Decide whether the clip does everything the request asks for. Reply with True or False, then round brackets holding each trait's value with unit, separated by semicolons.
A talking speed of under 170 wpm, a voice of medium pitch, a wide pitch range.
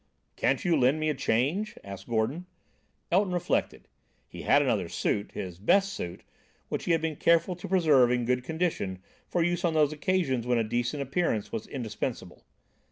False (175 wpm; 145 Hz; 6.7 semitones)